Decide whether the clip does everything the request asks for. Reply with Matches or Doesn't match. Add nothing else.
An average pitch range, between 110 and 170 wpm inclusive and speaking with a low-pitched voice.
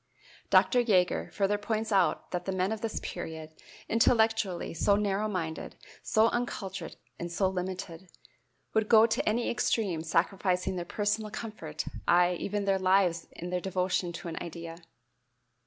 Doesn't match